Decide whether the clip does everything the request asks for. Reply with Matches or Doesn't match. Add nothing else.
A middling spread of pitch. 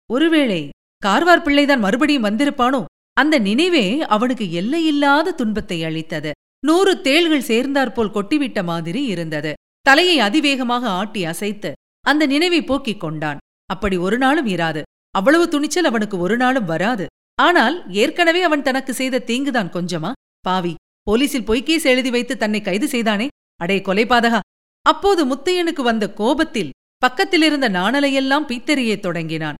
Doesn't match